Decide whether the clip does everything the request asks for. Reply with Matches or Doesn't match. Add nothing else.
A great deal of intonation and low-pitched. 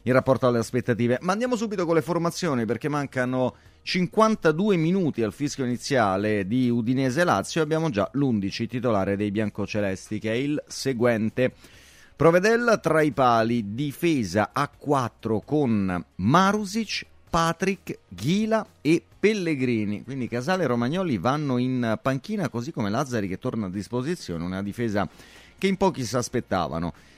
Matches